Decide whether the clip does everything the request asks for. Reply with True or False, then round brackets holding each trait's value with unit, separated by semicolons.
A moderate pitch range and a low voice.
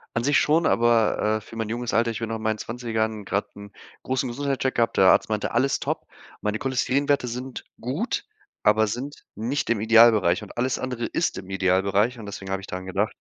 True (3.2 semitones; 115 Hz)